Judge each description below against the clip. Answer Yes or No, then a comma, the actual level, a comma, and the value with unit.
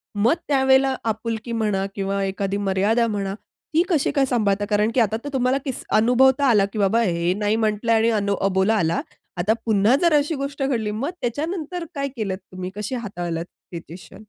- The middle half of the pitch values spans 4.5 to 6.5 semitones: Yes, average, 4.9 semitones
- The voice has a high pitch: Yes, high, 220 Hz